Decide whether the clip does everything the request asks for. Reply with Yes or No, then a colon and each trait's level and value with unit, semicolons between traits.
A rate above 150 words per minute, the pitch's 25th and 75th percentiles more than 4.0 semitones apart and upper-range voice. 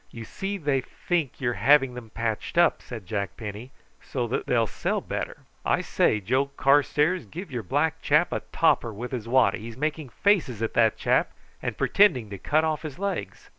No: average, 190 wpm; wide, 5.4 semitones; low, 130 Hz